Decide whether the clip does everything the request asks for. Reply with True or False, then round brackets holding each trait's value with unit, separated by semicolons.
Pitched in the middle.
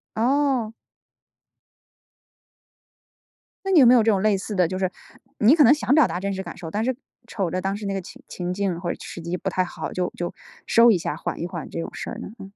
False (195 Hz)